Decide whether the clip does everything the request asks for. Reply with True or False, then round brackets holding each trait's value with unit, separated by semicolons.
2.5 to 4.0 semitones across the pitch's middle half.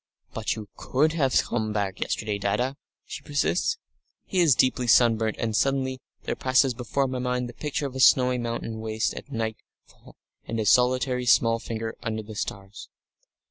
True (2.8 semitones)